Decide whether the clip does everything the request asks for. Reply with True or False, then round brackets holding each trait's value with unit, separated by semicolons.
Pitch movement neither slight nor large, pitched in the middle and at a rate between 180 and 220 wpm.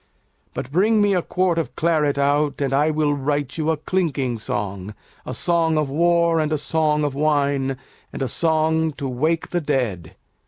True (3.1 semitones; 150 Hz; 185 wpm)